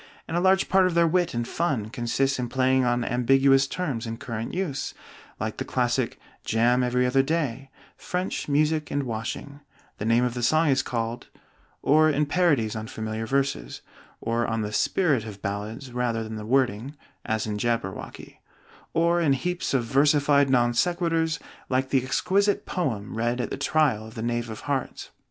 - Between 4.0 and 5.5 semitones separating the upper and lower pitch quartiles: Yes, average, 4.6 semitones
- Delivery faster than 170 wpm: Yes, average, 180 wpm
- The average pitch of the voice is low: Yes, low, 130 Hz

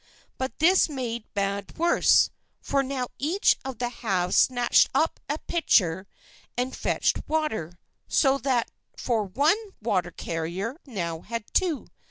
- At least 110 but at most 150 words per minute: Yes, average, 140 wpm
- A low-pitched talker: No, high, 245 Hz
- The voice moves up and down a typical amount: No, wide, 6.0 semitones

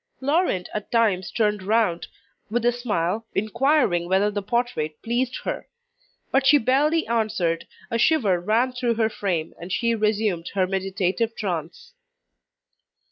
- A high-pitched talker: Yes, high, 215 Hz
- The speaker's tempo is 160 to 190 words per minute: No, slow, 135 wpm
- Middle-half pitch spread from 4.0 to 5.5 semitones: Yes, average, 4.5 semitones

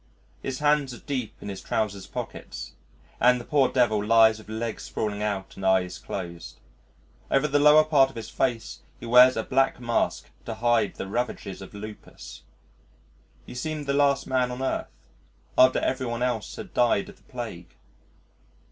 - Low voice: Yes, low, 120 Hz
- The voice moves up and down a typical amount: Yes, average, 3.8 semitones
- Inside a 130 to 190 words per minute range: Yes, average, 175 wpm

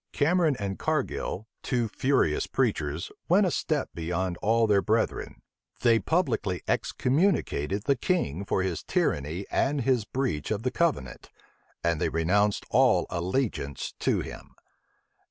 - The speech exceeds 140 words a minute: No, slow, 135 wpm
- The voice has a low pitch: Yes, low, 105 Hz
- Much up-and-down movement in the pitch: Yes, wide, 7.8 semitones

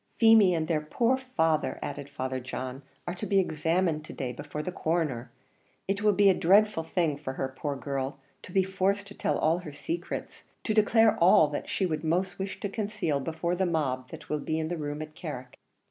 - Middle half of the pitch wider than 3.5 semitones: Yes, average, 4.7 semitones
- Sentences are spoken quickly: Yes, fast, 210 wpm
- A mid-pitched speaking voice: Yes, medium, 165 Hz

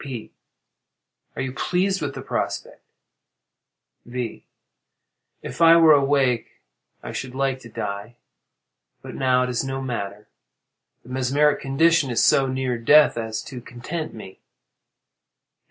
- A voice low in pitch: Yes, low, 130 Hz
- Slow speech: Yes, slow, 130 wpm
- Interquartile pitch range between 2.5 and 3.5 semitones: Yes, average, 3.2 semitones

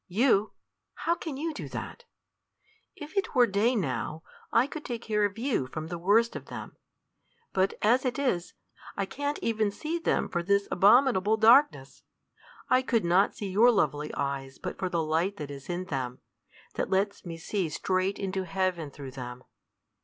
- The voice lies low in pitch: No, high, 195 Hz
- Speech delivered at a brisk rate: No, average, 175 wpm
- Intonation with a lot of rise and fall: Yes, wide, 6.2 semitones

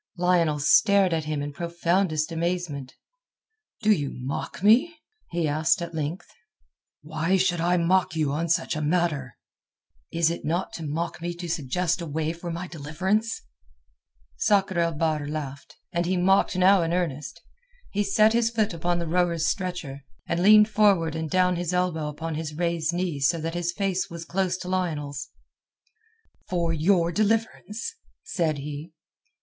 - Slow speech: No, average, 165 wpm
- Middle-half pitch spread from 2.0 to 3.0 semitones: Yes, average, 2.7 semitones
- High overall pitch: No, medium, 170 Hz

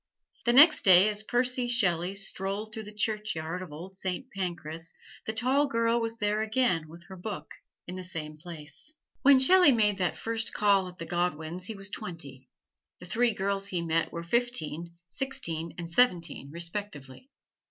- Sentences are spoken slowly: No, average, 170 wpm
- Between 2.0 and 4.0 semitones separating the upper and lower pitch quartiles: No, average, 5.1 semitones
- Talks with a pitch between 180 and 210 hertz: Yes, high, 190 Hz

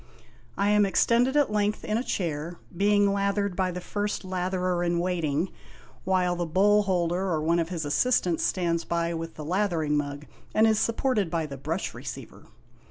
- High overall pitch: No, medium, 180 Hz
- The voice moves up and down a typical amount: Yes, average, 3.5 semitones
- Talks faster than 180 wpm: Yes, average, 195 wpm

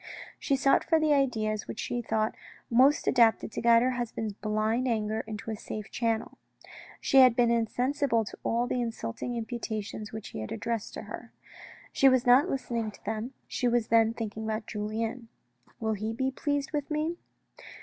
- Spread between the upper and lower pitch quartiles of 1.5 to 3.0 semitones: Yes, average, 2.7 semitones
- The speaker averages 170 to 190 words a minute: Yes, average, 180 wpm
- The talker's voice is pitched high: Yes, high, 230 Hz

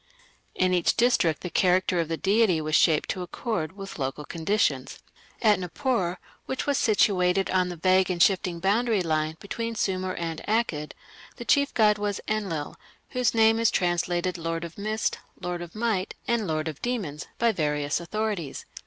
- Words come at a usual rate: Yes, average, 170 wpm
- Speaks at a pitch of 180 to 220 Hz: Yes, medium, 185 Hz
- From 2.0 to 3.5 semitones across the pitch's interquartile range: No, average, 4.5 semitones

